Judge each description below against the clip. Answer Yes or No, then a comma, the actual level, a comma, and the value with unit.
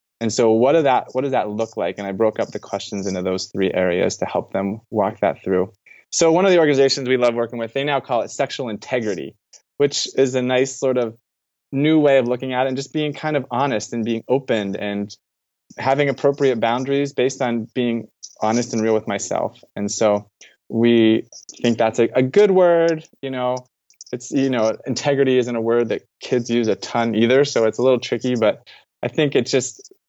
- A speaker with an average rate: No, fast, 215 wpm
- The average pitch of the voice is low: Yes, low, 120 Hz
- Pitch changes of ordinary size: Yes, average, 3.6 semitones